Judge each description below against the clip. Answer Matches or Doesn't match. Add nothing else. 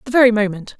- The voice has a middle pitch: Doesn't match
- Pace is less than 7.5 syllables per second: Doesn't match